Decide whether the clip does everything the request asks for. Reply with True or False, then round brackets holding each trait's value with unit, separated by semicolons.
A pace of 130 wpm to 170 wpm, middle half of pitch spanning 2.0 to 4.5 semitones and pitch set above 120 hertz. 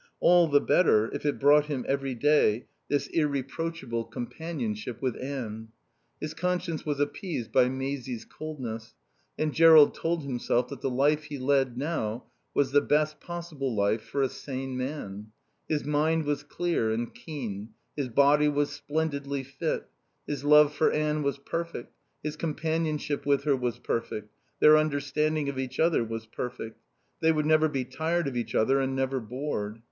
True (160 wpm; 3.4 semitones; 140 Hz)